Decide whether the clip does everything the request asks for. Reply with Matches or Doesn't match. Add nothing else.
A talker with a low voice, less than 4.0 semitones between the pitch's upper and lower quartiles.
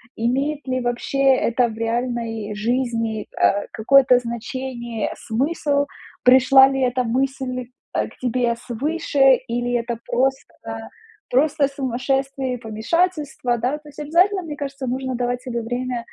Doesn't match